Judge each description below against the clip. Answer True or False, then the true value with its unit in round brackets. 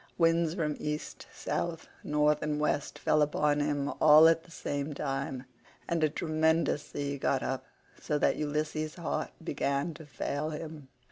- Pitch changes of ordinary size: False (1.7 semitones)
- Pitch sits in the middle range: True (150 Hz)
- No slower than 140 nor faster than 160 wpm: True (155 wpm)